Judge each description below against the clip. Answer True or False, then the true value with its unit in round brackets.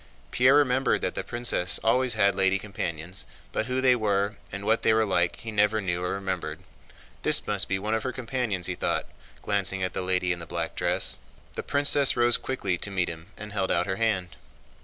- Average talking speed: False (210 wpm)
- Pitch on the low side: True (100 Hz)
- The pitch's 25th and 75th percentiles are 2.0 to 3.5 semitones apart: False (4.3 semitones)